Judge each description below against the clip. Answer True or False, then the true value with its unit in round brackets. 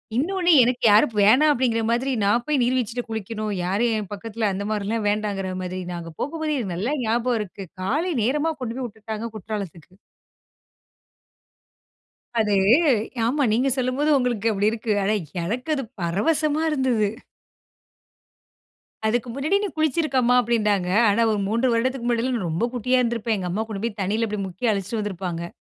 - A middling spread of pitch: True (3.8 semitones)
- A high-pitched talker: True (230 Hz)